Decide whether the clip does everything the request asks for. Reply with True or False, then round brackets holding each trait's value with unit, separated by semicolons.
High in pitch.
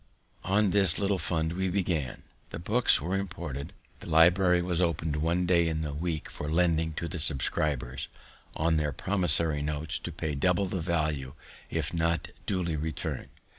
False (85 Hz)